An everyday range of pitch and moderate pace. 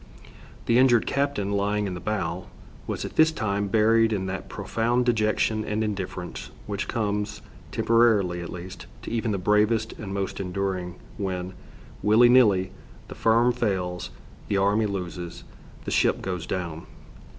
Yes: average, 3.3 semitones; average, 150 wpm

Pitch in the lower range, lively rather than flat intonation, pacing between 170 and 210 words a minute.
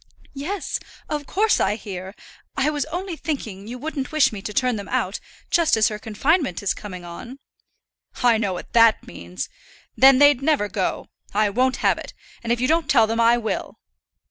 No: high, 240 Hz; wide, 5.7 semitones; average, 190 wpm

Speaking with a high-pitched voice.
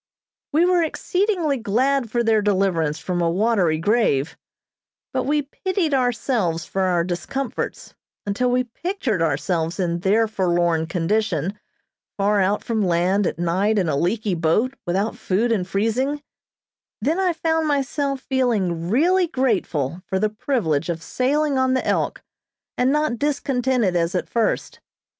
Yes: high, 215 Hz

